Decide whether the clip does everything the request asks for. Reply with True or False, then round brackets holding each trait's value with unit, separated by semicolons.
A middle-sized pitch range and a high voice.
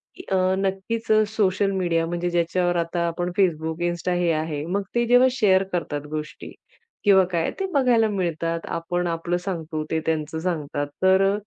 False (3.0 semitones; 175 Hz)